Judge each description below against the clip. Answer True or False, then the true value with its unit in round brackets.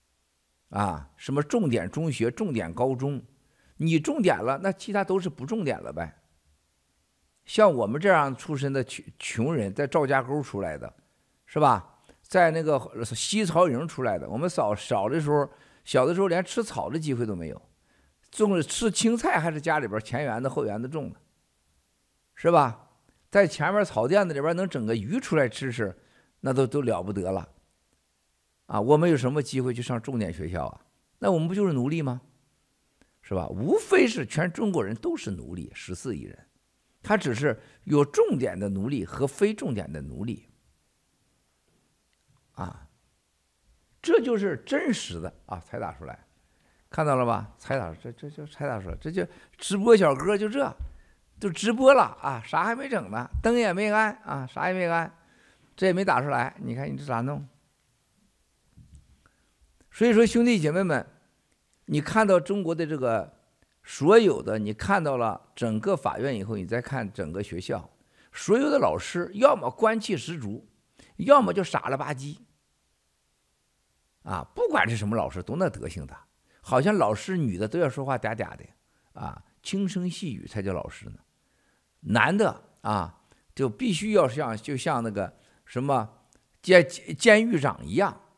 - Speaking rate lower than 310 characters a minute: True (235 characters per minute)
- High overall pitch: False (135 Hz)